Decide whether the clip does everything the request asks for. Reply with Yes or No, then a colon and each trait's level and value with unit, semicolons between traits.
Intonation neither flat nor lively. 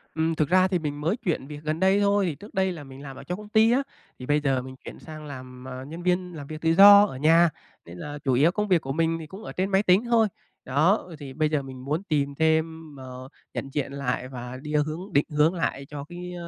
Yes: average, 4.6 semitones